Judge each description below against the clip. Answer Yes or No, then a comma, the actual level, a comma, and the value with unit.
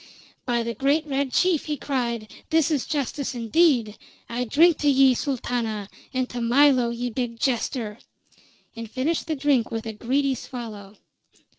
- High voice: Yes, very high, 250 Hz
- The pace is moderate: Yes, average, 155 wpm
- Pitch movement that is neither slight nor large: Yes, average, 3.5 semitones